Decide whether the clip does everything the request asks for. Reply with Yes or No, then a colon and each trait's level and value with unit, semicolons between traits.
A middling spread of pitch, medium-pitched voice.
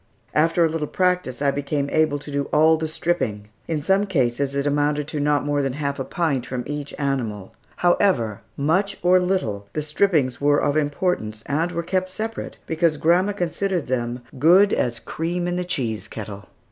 Yes: average, 4.4 semitones; medium, 150 Hz